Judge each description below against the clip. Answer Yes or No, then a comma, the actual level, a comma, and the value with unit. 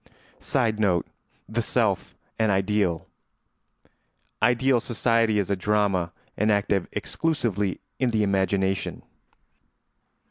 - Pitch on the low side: Yes, low, 105 Hz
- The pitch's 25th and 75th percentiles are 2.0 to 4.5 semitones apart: Yes, average, 2.9 semitones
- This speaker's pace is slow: Yes, slow, 85 wpm